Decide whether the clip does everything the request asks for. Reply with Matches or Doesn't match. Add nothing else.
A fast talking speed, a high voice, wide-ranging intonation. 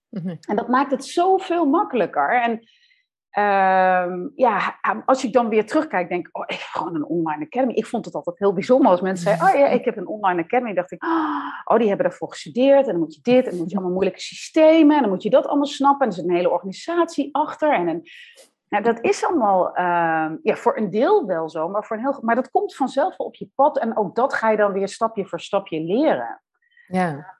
Matches